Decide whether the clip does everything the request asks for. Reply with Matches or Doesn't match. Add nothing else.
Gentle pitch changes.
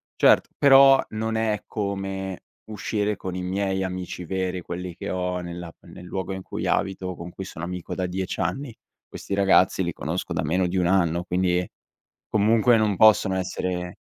Matches